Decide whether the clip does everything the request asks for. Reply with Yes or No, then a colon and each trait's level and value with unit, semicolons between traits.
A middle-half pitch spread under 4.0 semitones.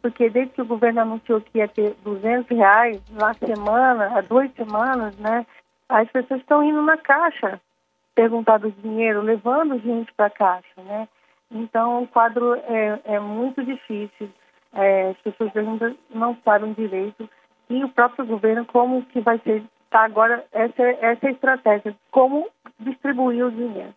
Yes: narrow, 2.6 semitones